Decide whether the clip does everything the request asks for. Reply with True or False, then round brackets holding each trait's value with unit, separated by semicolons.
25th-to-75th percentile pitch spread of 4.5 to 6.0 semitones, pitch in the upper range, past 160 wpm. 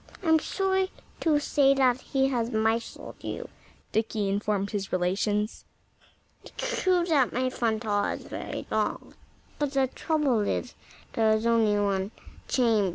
False (4.8 semitones; 235 Hz; 140 wpm)